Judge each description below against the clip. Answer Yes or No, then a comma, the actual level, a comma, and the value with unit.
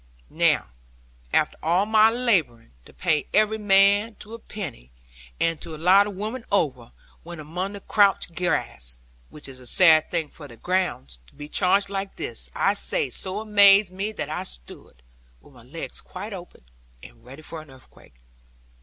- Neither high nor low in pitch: Yes, medium, 180 Hz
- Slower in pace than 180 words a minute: Yes, average, 170 wpm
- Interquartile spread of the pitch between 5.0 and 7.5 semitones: Yes, wide, 5.5 semitones